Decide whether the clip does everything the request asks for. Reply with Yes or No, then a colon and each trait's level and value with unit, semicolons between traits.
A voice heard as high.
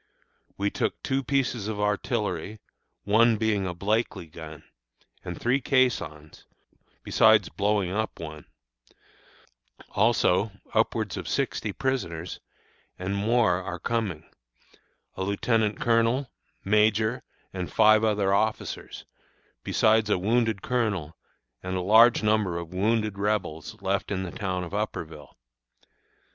No: low, 105 Hz